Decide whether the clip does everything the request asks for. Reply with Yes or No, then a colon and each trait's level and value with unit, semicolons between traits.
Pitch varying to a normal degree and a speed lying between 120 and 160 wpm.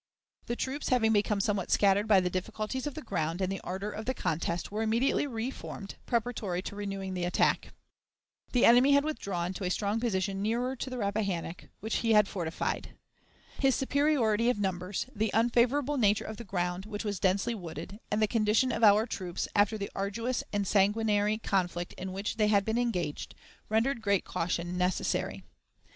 No: average, 3.4 semitones; average, 180 wpm